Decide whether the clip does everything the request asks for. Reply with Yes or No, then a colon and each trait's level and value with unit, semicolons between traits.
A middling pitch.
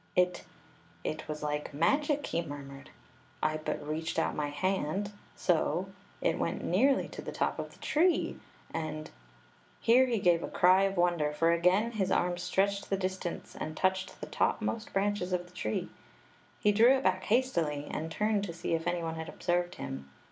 Yes: medium, 175 Hz